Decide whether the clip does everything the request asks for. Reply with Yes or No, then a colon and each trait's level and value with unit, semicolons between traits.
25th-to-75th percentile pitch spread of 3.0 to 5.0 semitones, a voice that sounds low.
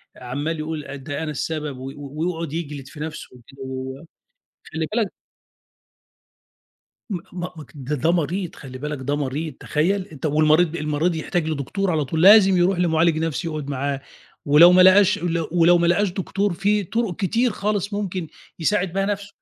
No: average, 3.9 semitones; medium, 165 Hz